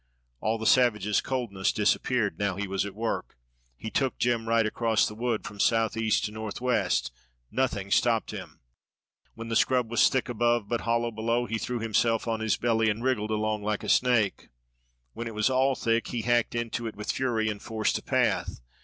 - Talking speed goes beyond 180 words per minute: Yes, average, 190 wpm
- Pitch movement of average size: No, narrow, 1.9 semitones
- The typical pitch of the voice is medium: No, low, 115 Hz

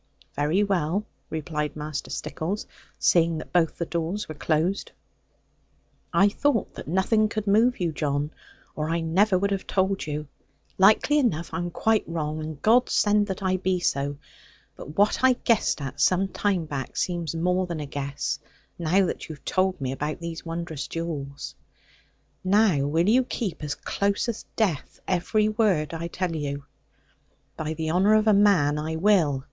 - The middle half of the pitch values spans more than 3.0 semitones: Yes, average, 4.6 semitones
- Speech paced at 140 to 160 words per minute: No, average, 170 wpm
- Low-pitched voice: No, medium, 170 Hz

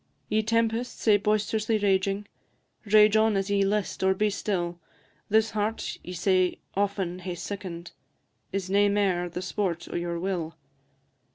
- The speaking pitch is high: Yes, high, 200 Hz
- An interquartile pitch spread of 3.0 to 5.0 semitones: No, narrow, 2.6 semitones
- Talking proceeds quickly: No, average, 150 wpm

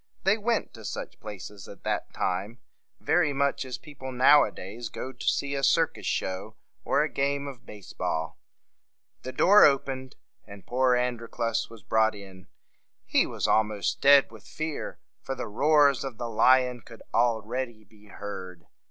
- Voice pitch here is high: No, low, 120 Hz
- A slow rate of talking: No, average, 170 wpm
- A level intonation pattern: No, average, 4.5 semitones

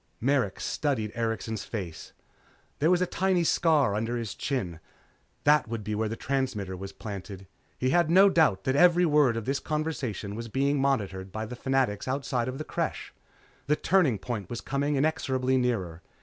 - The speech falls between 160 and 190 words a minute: Yes, average, 170 wpm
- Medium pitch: No, low, 125 Hz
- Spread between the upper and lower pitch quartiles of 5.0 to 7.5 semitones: Yes, wide, 5.4 semitones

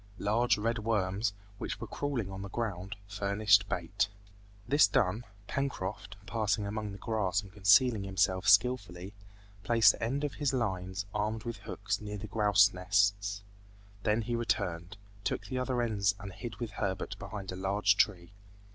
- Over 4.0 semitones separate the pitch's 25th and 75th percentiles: No, average, 2.7 semitones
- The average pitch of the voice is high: No, low, 105 Hz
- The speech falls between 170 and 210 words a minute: No, average, 160 wpm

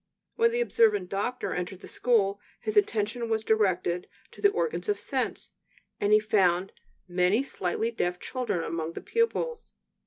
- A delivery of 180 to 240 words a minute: No, average, 155 wpm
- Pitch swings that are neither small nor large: No, wide, 5.9 semitones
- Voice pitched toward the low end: No, high, 215 Hz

